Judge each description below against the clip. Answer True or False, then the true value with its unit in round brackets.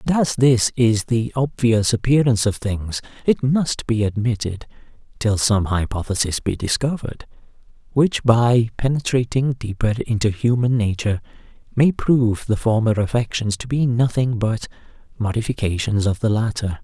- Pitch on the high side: False (115 Hz)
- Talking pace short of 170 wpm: True (135 wpm)